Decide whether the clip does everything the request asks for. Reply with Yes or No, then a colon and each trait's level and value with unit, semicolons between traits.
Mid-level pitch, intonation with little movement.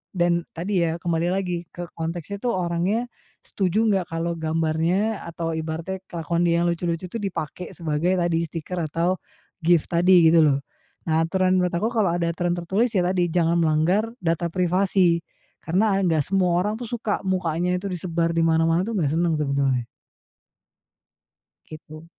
Yes: medium, 170 Hz; narrow, 2.2 semitones